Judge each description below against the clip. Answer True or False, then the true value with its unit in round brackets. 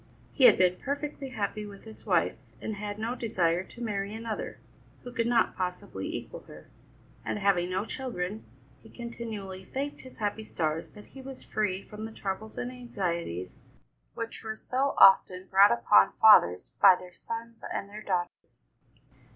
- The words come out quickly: False (165 wpm)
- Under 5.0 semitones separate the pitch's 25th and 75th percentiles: True (3.9 semitones)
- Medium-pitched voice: False (210 Hz)